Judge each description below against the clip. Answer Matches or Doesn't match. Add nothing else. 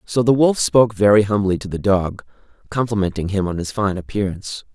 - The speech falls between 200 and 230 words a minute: Doesn't match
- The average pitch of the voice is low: Matches